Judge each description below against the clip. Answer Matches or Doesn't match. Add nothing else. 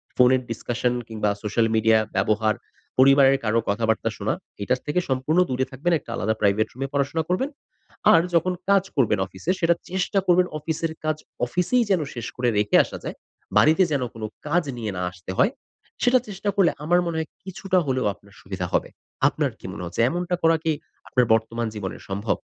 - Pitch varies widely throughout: Matches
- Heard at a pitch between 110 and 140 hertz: Matches